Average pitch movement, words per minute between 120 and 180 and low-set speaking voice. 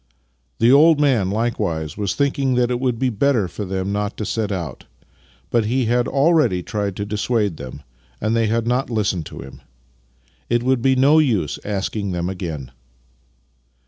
Yes: average, 4.9 semitones; average, 175 wpm; low, 110 Hz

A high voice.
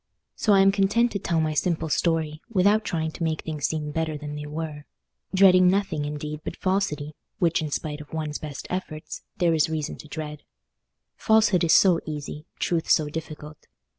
No: medium, 160 Hz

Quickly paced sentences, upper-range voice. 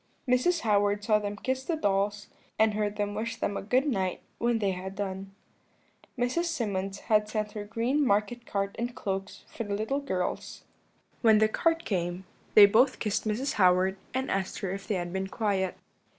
No: average, 185 wpm; high, 210 Hz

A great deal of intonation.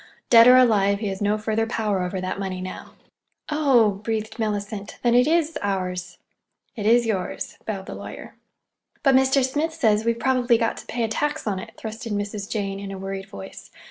No: average, 3.3 semitones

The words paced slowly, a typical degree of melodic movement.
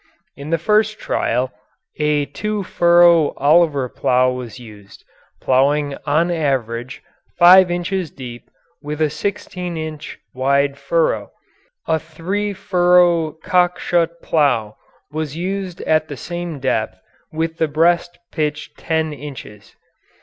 Yes: slow, 125 wpm; average, 3.9 semitones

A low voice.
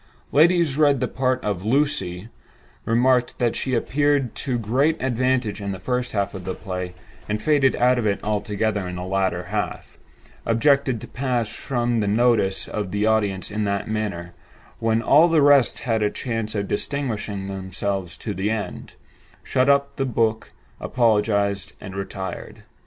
Yes: low, 110 Hz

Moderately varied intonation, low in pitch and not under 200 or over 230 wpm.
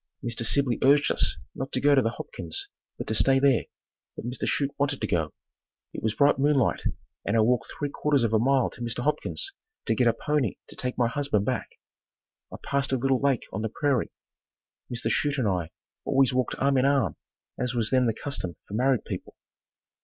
Yes: average, 3.4 semitones; low, 130 Hz; fast, 205 wpm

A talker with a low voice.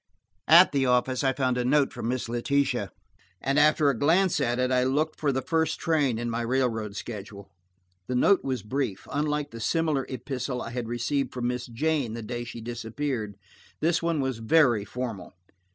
Yes: low, 125 Hz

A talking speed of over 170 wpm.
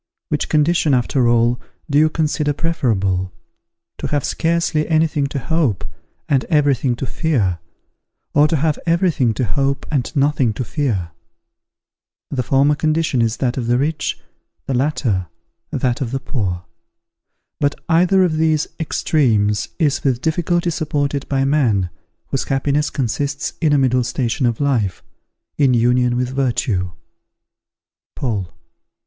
No: average, 145 wpm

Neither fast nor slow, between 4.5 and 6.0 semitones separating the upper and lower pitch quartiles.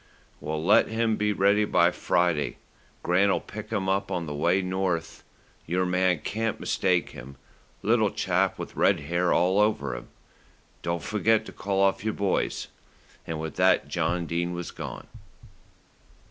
No: average, 155 wpm; average, 2.8 semitones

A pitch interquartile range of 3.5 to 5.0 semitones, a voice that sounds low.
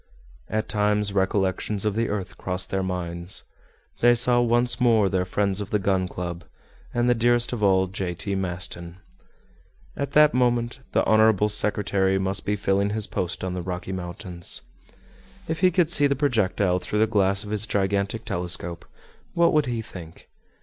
Yes: average, 3.8 semitones; low, 100 Hz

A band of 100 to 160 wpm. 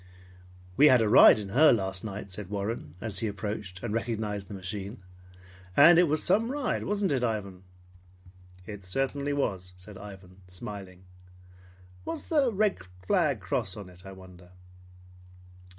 Yes: average, 150 wpm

